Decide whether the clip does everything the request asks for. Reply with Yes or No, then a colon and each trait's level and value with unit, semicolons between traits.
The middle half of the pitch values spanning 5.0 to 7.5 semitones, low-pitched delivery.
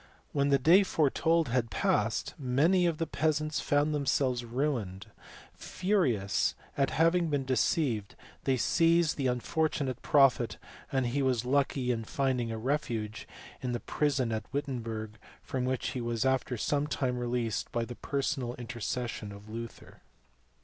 No: average, 3.7 semitones; low, 130 Hz